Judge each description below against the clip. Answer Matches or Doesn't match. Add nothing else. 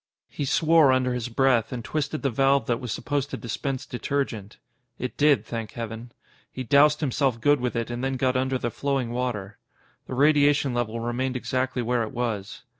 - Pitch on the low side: Matches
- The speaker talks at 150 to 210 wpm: Matches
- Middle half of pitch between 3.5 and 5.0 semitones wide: Doesn't match